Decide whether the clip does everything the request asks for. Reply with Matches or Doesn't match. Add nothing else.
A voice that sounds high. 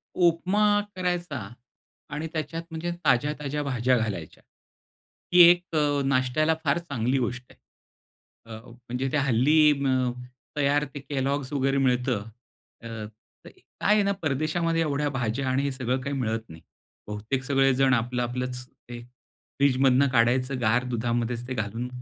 Doesn't match